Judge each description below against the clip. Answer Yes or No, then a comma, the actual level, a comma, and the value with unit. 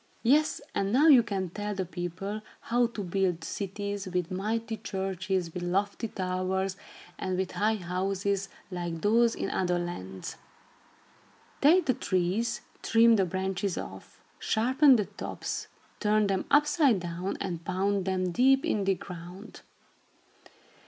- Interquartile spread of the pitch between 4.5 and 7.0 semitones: No, average, 3.3 semitones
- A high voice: Yes, high, 195 Hz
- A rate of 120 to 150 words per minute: Yes, average, 140 wpm